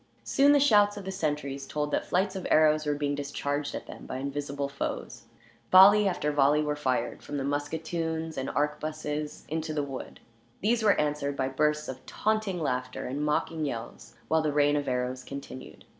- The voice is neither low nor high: Yes, medium, 150 Hz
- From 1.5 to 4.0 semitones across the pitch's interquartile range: Yes, narrow, 2.5 semitones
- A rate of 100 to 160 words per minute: No, average, 185 wpm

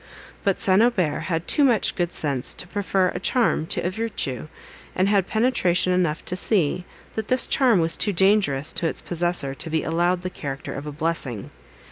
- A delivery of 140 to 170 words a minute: No, average, 190 wpm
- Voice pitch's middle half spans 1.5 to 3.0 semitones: No, average, 4.1 semitones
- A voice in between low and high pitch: Yes, medium, 180 Hz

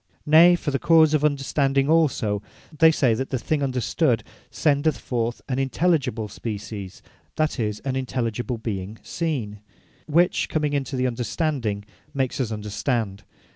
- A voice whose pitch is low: Yes, low, 130 Hz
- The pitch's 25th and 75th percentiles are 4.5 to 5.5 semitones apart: Yes, average, 5.1 semitones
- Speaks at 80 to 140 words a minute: Yes, slow, 135 wpm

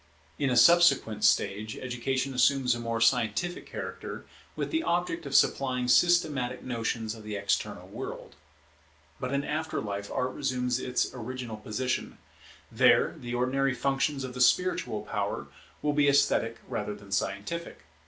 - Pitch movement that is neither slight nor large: Yes, average, 3.4 semitones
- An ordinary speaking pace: Yes, average, 145 wpm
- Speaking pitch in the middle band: No, low, 125 Hz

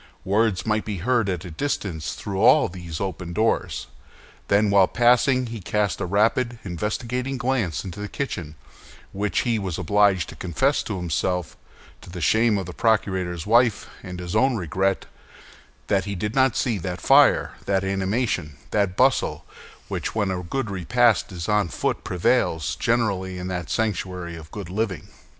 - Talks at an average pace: Yes, average, 170 wpm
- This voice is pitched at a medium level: No, low, 100 Hz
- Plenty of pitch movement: No, average, 4.0 semitones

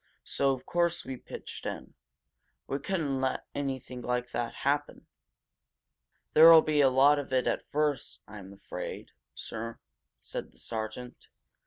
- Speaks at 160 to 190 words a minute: No, average, 140 wpm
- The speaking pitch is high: No, low, 135 Hz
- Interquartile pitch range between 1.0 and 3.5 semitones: Yes, average, 3.1 semitones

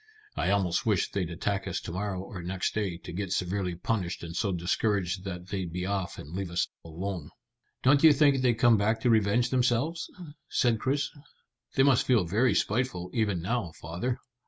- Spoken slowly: No, average, 185 wpm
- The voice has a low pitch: Yes, low, 100 Hz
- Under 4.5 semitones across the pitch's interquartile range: No, average, 5.0 semitones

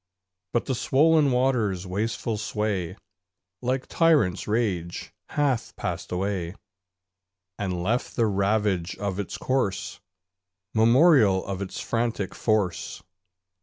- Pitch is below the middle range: Yes, low, 105 Hz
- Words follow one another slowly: Yes, slow, 105 wpm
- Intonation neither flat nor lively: Yes, average, 4.5 semitones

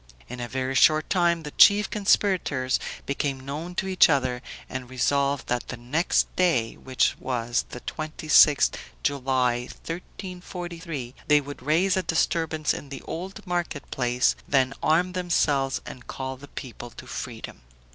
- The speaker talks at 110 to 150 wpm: Yes, average, 145 wpm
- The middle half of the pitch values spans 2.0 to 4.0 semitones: No, average, 4.8 semitones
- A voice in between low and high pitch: Yes, medium, 145 Hz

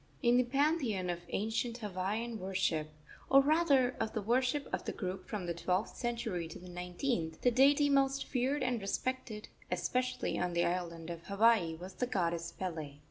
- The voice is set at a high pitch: Yes, high, 215 Hz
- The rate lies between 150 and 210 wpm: Yes, average, 175 wpm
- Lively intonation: Yes, wide, 6.1 semitones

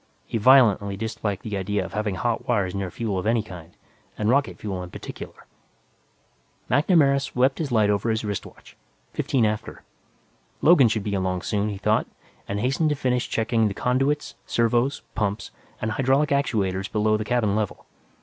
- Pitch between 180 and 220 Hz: No, low, 110 Hz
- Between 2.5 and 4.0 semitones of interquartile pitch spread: Yes, average, 3.7 semitones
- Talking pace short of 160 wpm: No, average, 170 wpm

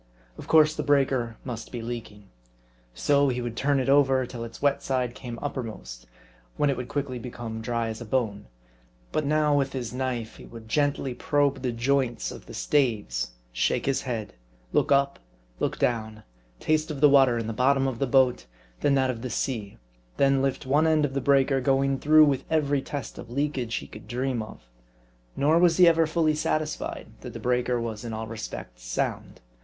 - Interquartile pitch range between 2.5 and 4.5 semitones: Yes, average, 3.5 semitones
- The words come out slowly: No, average, 195 wpm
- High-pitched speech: No, low, 130 Hz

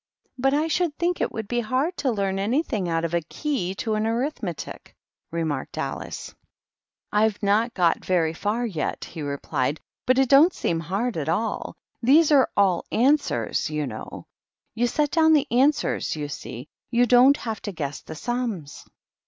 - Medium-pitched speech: No, high, 220 Hz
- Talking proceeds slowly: No, average, 185 wpm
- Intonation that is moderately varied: No, wide, 8.0 semitones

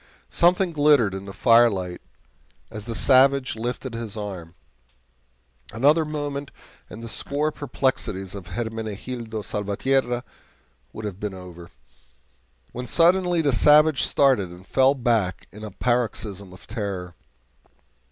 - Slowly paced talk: Yes, slow, 125 wpm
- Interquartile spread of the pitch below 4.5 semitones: No, wide, 5.4 semitones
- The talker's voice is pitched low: Yes, low, 115 Hz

